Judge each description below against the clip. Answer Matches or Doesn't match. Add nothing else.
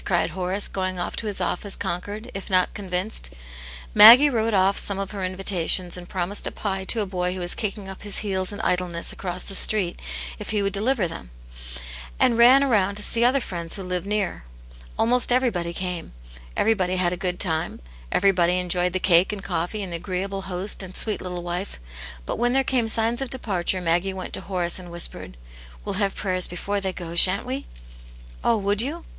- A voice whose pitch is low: Doesn't match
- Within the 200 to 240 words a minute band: Matches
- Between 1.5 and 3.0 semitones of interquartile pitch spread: Matches